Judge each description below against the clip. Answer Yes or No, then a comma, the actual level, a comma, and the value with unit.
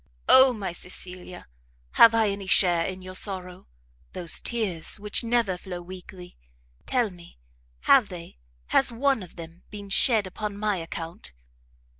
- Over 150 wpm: No, average, 145 wpm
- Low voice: No, high, 190 Hz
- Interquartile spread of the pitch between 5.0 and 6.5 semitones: No, average, 3.5 semitones